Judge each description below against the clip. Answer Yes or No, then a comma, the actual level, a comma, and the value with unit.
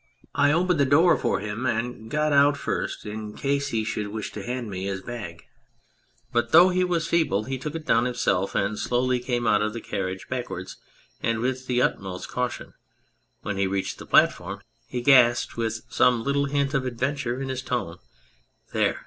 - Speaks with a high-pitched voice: No, low, 120 Hz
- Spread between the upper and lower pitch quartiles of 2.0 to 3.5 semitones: No, average, 4.6 semitones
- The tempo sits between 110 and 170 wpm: No, average, 195 wpm